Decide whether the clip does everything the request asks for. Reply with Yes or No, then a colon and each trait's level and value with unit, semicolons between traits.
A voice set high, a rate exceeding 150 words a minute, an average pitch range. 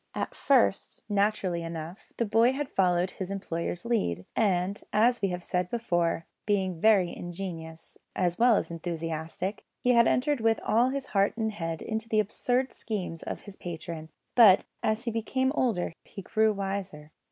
Yes: high, 195 Hz; average, 165 wpm; average, 4.5 semitones